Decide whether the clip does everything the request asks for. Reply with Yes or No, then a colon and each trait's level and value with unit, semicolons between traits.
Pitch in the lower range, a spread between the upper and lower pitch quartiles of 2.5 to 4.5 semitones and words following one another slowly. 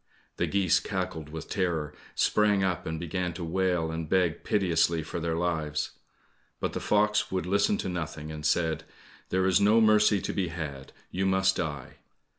No: very low, 90 Hz; average, 2.9 semitones; average, 175 wpm